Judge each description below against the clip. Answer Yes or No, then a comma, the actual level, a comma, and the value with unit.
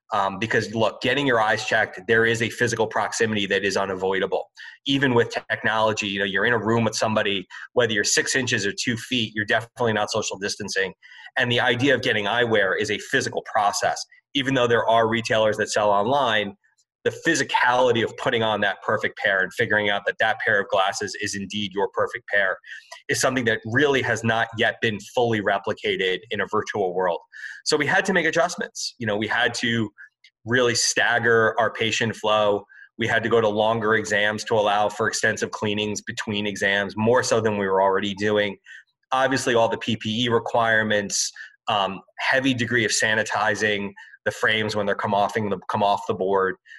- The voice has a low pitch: Yes, low, 110 Hz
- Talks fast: No, average, 190 wpm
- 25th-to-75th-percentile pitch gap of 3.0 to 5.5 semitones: No, narrow, 2.6 semitones